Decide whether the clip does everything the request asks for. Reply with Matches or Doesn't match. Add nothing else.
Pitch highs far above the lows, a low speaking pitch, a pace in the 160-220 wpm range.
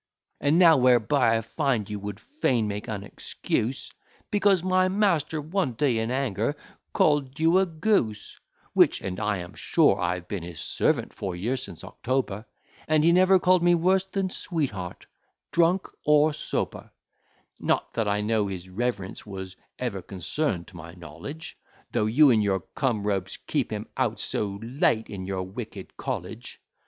Matches